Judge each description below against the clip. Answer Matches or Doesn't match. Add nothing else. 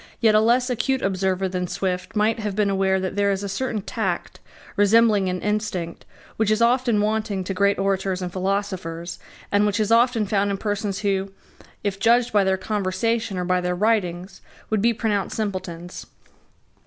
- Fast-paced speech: Doesn't match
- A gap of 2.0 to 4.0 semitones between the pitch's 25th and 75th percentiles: Matches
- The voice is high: Matches